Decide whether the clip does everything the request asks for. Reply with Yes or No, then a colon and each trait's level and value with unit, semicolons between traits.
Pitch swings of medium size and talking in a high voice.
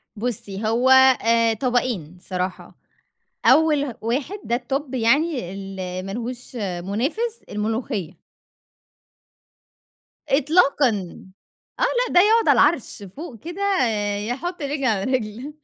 No: wide, 6.0 semitones; high, 245 Hz